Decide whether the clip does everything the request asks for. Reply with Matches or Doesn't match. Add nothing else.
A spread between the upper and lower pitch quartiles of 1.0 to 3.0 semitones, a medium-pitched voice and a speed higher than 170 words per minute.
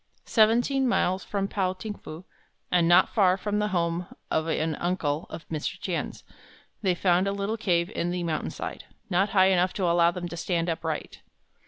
Matches